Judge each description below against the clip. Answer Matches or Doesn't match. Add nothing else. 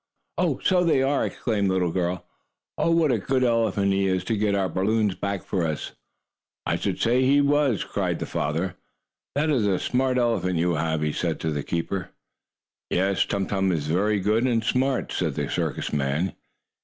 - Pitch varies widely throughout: Matches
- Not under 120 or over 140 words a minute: Doesn't match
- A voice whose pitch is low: Matches